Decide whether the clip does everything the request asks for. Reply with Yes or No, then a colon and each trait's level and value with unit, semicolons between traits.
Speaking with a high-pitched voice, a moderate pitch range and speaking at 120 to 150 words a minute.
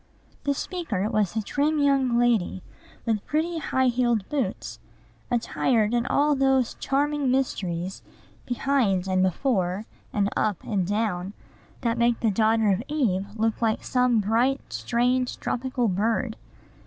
Yes: high, 235 Hz; average, 4.4 semitones; slow, 135 wpm